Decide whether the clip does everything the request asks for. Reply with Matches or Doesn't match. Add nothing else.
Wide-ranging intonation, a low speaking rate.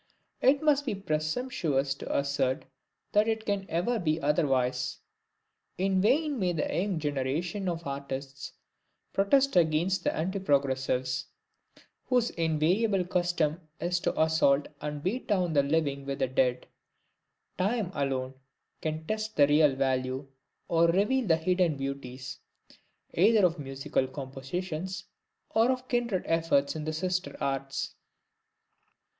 Matches